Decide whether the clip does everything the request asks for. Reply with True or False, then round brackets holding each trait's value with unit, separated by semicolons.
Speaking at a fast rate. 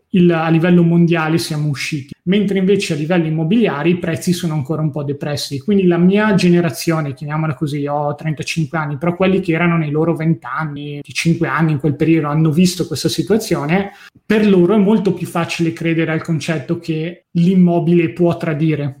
True (185 wpm)